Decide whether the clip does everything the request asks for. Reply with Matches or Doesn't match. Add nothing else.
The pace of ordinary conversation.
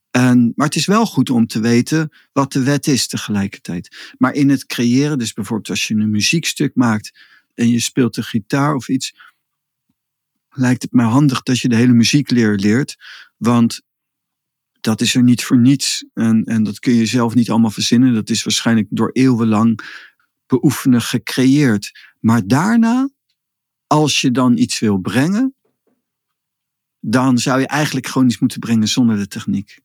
Matches